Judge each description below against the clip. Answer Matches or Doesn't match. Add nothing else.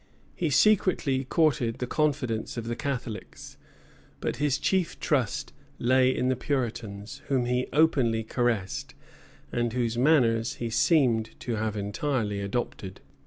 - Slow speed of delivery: Matches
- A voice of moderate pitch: Doesn't match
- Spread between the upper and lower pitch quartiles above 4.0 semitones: Doesn't match